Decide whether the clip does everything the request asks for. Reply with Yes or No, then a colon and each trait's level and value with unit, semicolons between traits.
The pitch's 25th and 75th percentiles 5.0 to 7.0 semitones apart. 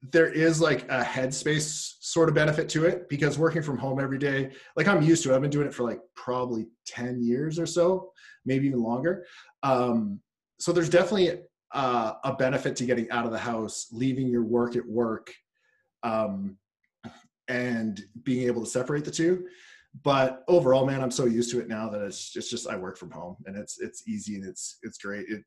Yes: average, 5.3 semitones